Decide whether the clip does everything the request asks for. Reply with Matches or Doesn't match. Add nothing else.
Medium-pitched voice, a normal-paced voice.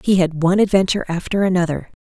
Matches